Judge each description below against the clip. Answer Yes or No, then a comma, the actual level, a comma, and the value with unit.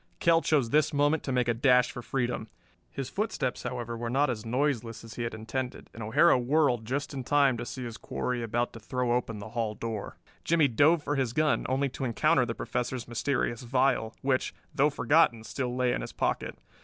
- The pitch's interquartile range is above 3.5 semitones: No, average, 3.2 semitones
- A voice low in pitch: Yes, low, 125 Hz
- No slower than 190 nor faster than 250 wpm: Yes, fast, 205 wpm